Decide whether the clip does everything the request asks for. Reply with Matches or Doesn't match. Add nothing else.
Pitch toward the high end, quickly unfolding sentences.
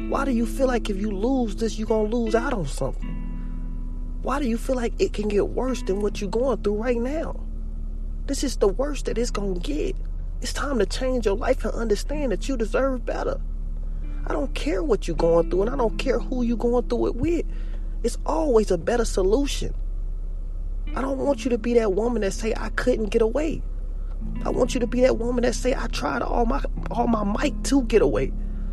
Matches